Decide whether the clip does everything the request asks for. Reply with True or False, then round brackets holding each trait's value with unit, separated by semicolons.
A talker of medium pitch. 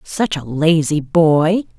True (165 Hz)